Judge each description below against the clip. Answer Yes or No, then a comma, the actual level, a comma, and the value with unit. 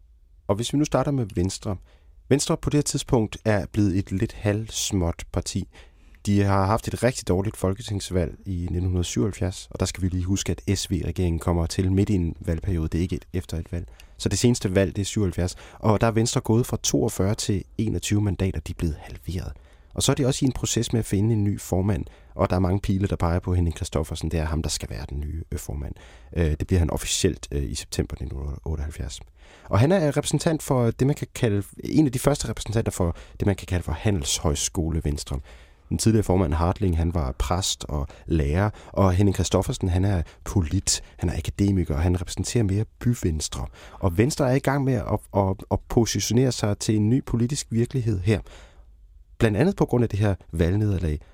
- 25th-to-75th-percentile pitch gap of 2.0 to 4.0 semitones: No, average, 4.9 semitones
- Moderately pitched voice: No, very low, 95 Hz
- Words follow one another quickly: No, average, 210 wpm